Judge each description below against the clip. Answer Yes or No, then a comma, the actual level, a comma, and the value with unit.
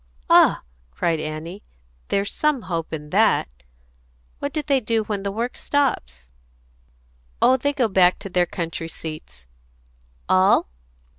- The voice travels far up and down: Yes, wide, 6.7 semitones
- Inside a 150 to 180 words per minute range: No, slow, 135 wpm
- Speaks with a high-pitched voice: Yes, high, 195 Hz